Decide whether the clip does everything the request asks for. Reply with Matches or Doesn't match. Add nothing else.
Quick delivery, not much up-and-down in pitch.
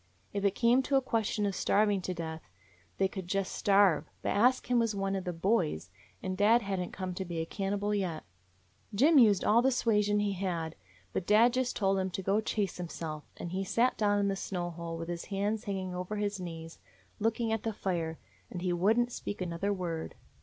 Doesn't match